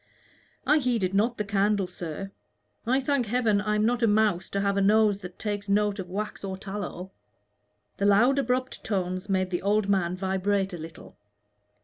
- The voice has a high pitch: Yes, high, 200 Hz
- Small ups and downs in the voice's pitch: Yes, narrow, 2.2 semitones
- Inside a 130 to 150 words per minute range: No, average, 180 wpm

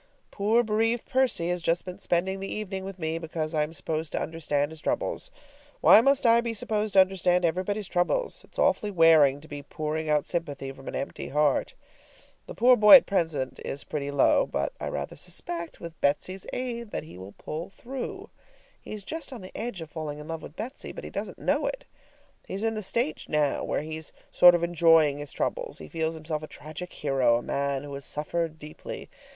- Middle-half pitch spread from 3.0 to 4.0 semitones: No, average, 5.2 semitones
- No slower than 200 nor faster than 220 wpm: Yes, fast, 205 wpm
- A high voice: No, medium, 165 Hz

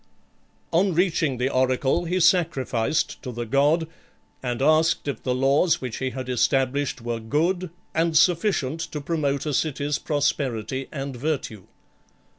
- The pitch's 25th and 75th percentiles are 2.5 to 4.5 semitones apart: Yes, average, 4.0 semitones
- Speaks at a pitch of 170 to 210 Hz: No, medium, 140 Hz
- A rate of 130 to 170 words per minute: Yes, slow, 135 wpm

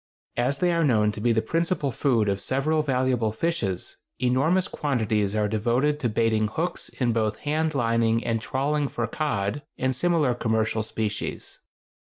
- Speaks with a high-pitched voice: No, low, 120 Hz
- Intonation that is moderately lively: Yes, average, 4.9 semitones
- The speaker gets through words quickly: No, average, 160 wpm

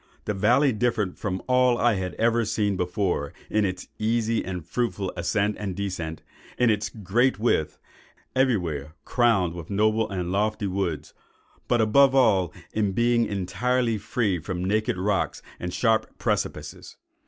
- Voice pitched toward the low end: Yes, low, 105 Hz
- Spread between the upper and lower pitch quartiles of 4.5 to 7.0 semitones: No, average, 3.9 semitones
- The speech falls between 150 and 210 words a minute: No, average, 140 wpm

